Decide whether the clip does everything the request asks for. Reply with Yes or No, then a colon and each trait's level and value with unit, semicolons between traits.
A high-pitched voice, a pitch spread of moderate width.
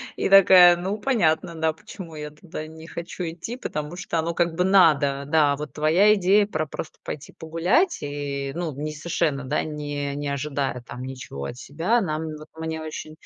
No: medium, 160 Hz; average, 3.2 semitones